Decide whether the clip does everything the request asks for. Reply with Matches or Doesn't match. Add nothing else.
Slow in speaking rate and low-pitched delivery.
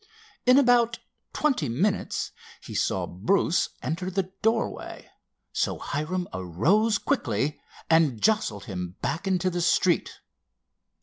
Doesn't match